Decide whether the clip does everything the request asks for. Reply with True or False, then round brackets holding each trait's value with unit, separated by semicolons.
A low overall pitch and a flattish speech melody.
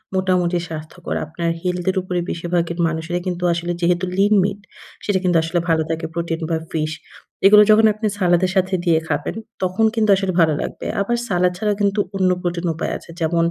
False (175 Hz; 2.1 semitones)